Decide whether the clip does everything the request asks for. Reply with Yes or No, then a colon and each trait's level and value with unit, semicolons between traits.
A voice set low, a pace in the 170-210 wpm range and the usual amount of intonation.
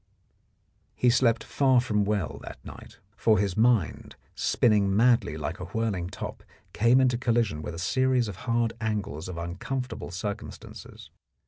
No: low, 110 Hz; average, 145 wpm; average, 4.4 semitones